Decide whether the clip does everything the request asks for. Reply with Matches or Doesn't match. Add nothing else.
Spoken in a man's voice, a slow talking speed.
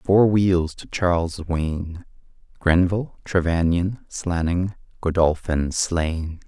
Matches